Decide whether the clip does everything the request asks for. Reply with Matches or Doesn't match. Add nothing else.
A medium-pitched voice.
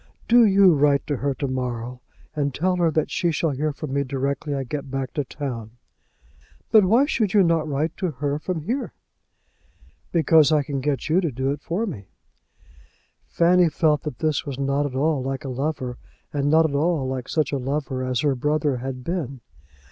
Matches